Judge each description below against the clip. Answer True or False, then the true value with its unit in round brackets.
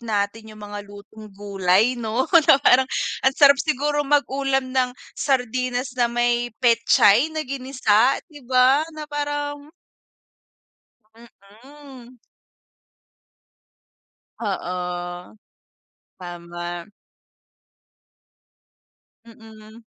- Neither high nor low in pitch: False (240 Hz)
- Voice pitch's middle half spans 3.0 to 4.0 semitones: False (4.7 semitones)